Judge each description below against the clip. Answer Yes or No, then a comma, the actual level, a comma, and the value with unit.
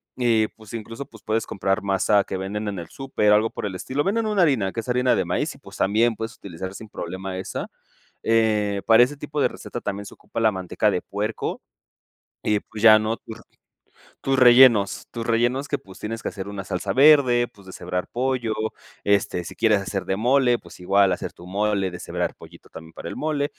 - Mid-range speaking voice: No, low, 110 Hz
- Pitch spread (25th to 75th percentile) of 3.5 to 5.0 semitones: Yes, average, 3.8 semitones